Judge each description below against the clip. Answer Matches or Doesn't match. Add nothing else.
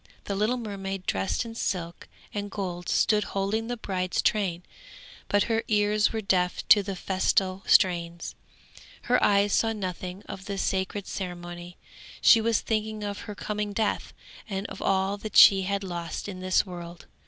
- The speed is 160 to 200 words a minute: Matches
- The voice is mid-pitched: Doesn't match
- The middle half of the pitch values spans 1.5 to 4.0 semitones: Matches